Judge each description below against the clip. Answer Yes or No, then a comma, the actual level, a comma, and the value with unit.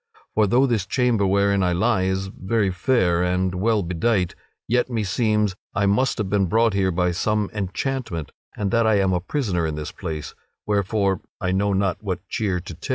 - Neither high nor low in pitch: No, low, 100 Hz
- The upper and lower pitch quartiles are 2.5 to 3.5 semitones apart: Yes, average, 3.1 semitones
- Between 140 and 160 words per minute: No, average, 190 wpm